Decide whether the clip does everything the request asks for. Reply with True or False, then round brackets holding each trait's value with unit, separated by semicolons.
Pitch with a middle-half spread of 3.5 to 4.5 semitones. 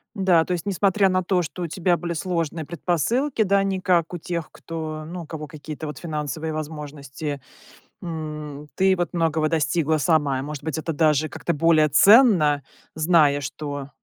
False (2.8 semitones)